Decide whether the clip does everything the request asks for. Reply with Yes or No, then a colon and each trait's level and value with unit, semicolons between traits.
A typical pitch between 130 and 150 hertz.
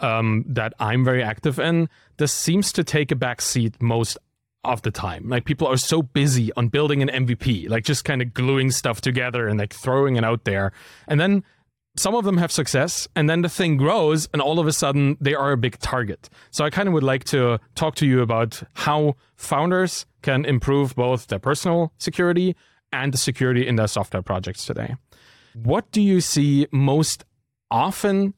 Yes: low, 135 Hz